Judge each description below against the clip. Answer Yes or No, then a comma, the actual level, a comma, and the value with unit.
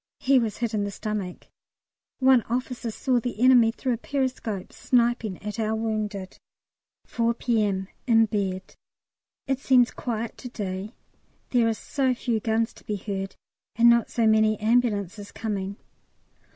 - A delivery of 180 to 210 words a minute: No, average, 150 wpm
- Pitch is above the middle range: Yes, high, 225 Hz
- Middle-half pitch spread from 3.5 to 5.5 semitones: No, average, 2.8 semitones